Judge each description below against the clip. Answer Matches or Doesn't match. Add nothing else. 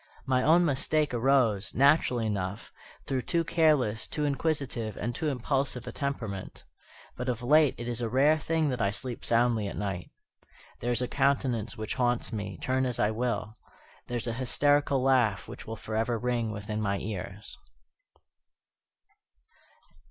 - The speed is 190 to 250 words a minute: Doesn't match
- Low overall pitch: Matches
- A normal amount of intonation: Matches